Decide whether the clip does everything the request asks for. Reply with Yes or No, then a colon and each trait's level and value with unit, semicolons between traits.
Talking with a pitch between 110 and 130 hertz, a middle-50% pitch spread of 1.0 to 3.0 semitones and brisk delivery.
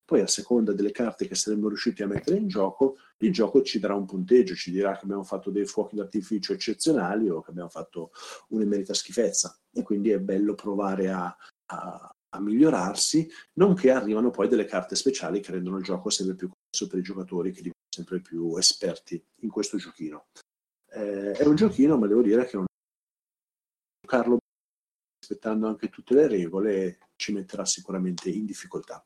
No: low, 100 Hz; average, 2.7 semitones; fast, 180 wpm